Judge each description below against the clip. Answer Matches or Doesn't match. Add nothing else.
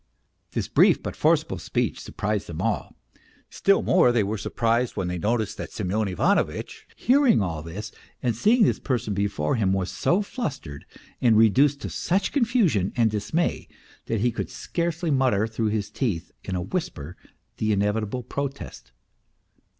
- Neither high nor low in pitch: Doesn't match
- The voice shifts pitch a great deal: Matches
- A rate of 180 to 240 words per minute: Doesn't match